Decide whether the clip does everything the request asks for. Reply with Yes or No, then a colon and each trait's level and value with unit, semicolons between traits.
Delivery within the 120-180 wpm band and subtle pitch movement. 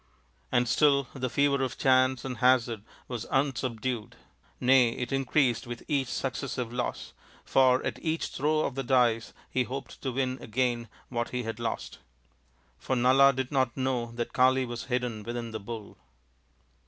Yes: average, 165 wpm; narrow, 1.9 semitones